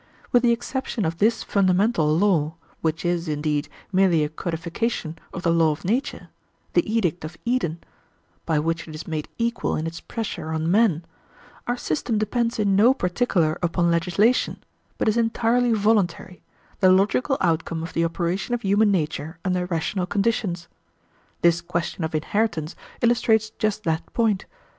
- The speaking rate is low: No, average, 155 wpm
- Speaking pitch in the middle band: Yes, medium, 180 Hz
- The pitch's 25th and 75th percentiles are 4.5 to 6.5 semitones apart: Yes, average, 5.1 semitones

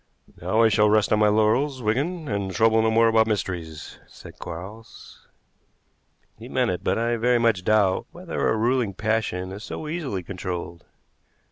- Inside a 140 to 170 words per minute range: Yes, average, 165 wpm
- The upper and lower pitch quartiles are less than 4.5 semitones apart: Yes, average, 3.2 semitones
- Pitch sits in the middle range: No, low, 110 Hz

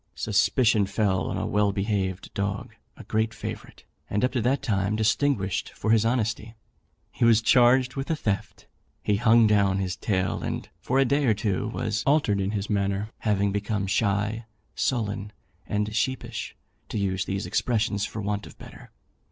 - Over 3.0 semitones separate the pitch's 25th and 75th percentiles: No, narrow, 2.5 semitones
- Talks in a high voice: No, low, 105 Hz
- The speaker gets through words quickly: No, average, 170 wpm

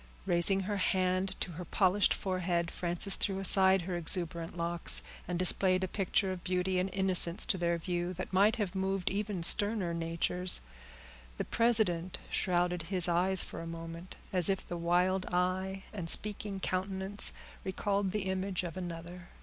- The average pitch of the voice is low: No, medium, 185 Hz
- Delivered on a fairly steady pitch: Yes, narrow, 1.8 semitones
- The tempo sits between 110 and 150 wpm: No, average, 160 wpm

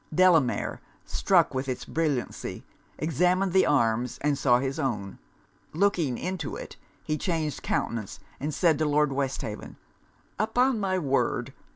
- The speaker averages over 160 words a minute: No, slow, 135 wpm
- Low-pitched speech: No, medium, 150 Hz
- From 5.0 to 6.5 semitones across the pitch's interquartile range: Yes, average, 5.3 semitones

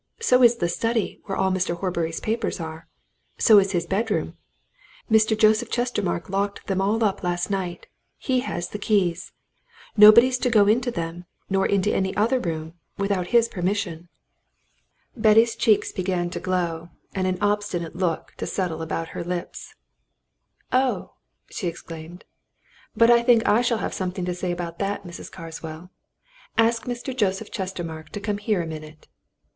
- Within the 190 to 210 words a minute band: No, average, 160 wpm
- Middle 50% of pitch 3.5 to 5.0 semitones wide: Yes, average, 4.0 semitones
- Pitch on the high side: Yes, high, 195 Hz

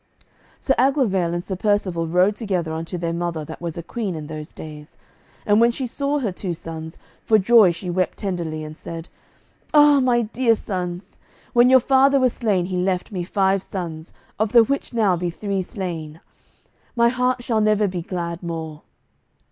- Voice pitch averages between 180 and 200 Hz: Yes, medium, 185 Hz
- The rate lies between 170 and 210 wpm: Yes, average, 180 wpm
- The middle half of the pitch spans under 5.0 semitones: No, average, 5.3 semitones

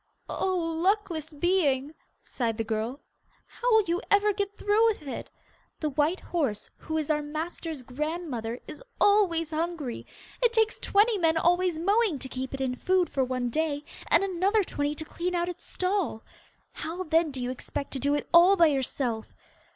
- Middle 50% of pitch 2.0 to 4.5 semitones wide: No, average, 5.0 semitones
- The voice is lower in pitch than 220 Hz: No, very high, 320 Hz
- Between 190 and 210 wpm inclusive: No, average, 175 wpm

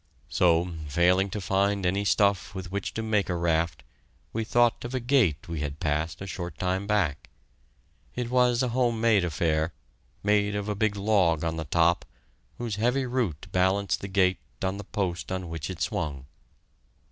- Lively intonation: No, average, 4.0 semitones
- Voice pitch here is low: Yes, very low, 95 Hz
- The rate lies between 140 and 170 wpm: No, average, 180 wpm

